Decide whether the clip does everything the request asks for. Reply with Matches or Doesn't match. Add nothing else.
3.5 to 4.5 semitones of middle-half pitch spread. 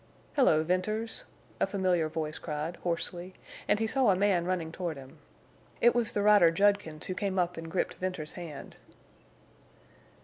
Matches